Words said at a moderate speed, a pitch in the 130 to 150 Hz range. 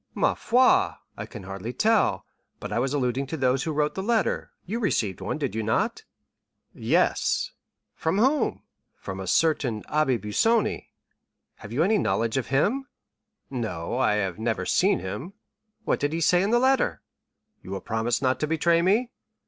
Yes: average, 175 wpm; medium, 140 Hz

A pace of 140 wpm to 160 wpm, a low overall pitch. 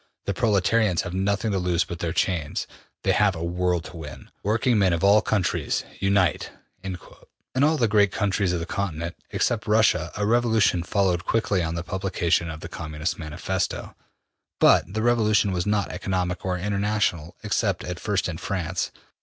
No: average, 170 wpm; very low, 95 Hz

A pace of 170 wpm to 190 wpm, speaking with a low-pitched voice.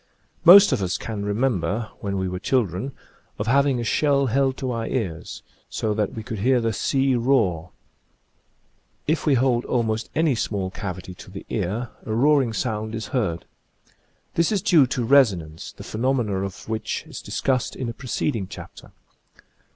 Yes: average, 175 wpm; low, 115 Hz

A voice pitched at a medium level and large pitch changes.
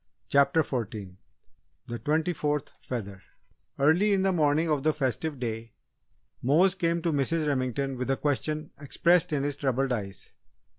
No: medium, 145 Hz; average, 3.9 semitones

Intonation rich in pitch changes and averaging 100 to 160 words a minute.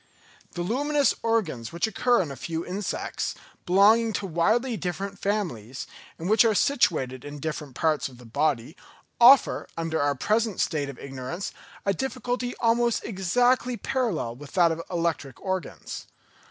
Yes: wide, 7.5 semitones; average, 155 wpm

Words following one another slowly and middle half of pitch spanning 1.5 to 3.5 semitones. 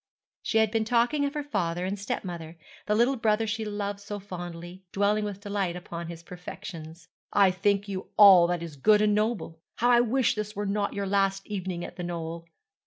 No: average, 200 wpm; average, 3.2 semitones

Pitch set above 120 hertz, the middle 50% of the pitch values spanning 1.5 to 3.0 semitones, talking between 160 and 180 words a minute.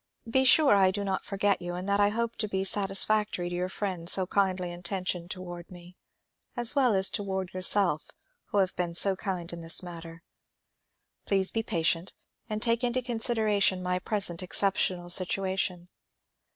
Yes: high, 190 Hz; narrow, 2.6 semitones; average, 170 wpm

